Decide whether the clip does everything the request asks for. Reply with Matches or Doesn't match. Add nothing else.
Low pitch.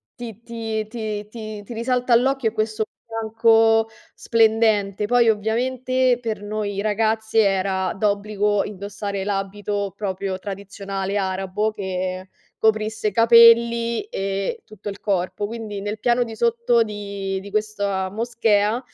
Doesn't match